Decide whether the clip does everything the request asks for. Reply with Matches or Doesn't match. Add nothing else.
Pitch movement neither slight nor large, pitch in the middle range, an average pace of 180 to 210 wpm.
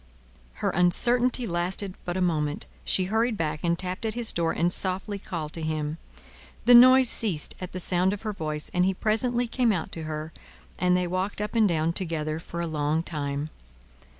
Matches